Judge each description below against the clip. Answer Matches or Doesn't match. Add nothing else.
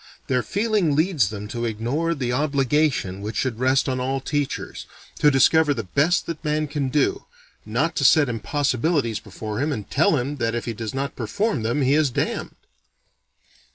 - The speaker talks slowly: Doesn't match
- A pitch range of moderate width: Matches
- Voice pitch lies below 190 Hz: Matches